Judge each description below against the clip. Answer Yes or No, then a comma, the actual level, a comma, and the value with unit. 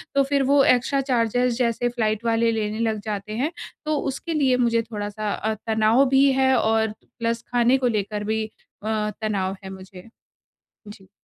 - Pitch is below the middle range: No, high, 230 Hz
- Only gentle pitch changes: No, average, 3.2 semitones